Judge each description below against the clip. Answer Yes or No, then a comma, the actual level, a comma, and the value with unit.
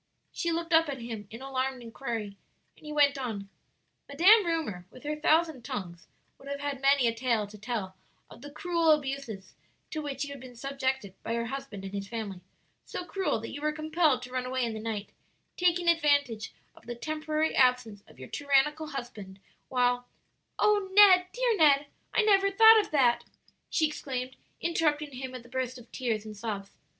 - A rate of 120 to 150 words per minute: No, average, 190 wpm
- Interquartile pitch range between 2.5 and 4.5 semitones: No, average, 4.9 semitones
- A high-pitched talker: Yes, very high, 270 Hz